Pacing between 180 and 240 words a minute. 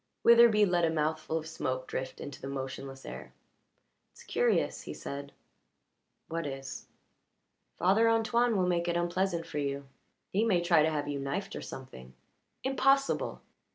No: average, 155 wpm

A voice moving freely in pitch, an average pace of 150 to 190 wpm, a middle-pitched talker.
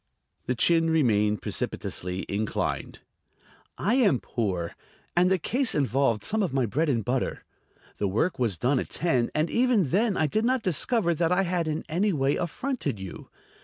Yes: wide, 8.0 semitones; average, 170 wpm; medium, 155 Hz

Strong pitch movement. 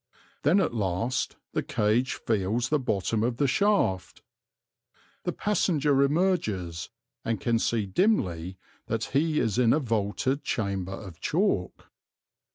Yes: wide, 6.9 semitones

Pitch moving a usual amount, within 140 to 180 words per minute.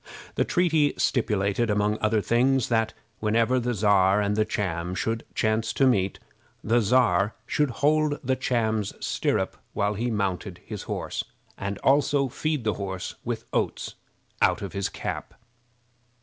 Yes: average, 3.9 semitones; average, 150 wpm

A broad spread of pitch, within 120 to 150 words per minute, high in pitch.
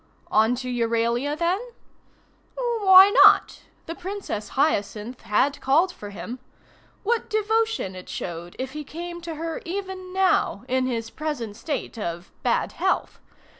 Yes: wide, 8.4 semitones; slow, 135 wpm; very high, 290 Hz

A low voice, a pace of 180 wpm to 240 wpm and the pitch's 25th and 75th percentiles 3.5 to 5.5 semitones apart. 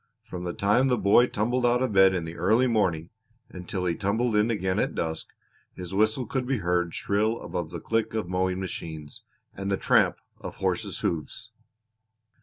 Yes: very low, 95 Hz; average, 185 wpm; average, 4.2 semitones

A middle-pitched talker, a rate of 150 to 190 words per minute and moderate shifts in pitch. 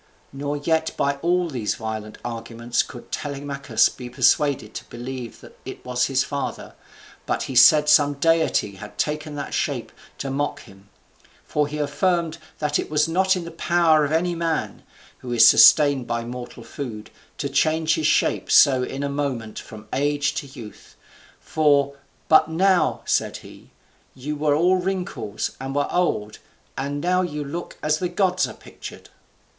Yes: medium, 145 Hz; average, 165 wpm; average, 4.0 semitones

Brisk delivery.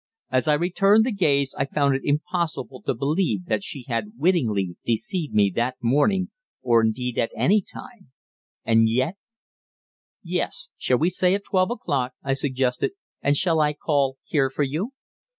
No: average, 165 wpm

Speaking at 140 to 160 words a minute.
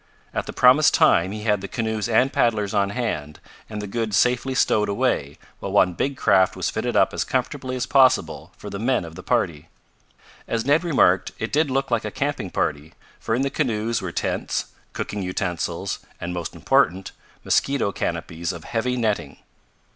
No: average, 185 wpm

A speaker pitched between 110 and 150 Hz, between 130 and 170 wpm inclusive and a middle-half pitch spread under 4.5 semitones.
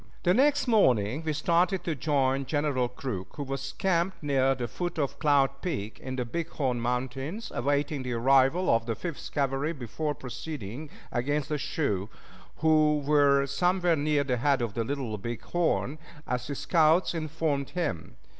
Yes: medium, 140 Hz; average, 165 wpm; average, 3.8 semitones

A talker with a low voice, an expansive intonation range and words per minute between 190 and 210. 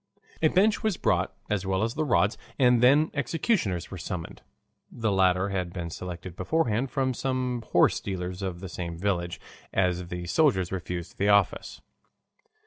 No: very low, 95 Hz; wide, 6.1 semitones; average, 160 wpm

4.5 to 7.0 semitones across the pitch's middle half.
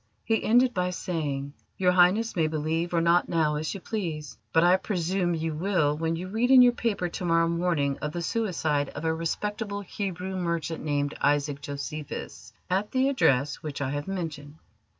No: average, 4.0 semitones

